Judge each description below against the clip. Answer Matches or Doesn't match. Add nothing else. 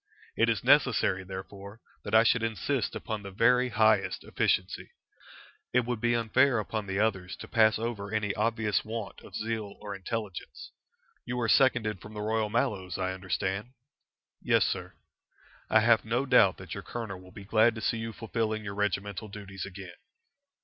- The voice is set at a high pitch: Doesn't match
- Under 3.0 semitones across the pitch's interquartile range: Matches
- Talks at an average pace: Matches